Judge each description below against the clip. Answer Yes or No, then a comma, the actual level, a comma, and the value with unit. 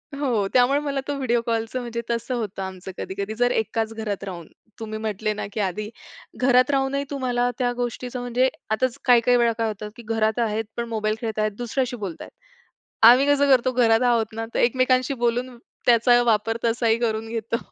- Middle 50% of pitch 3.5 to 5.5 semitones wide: No, narrow, 2.4 semitones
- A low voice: No, high, 235 Hz